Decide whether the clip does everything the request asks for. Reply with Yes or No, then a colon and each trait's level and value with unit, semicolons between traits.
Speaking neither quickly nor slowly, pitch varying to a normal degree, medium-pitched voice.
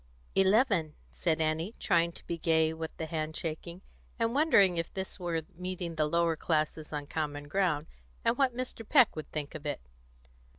Yes: average, 175 wpm; average, 3.4 semitones; medium, 165 Hz